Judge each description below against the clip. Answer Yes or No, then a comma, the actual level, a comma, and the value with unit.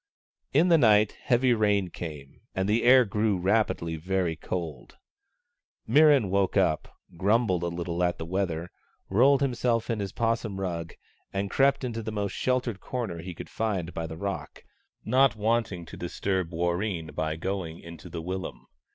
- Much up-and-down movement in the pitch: No, average, 4.9 semitones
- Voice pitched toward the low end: Yes, very low, 95 Hz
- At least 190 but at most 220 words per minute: No, average, 160 wpm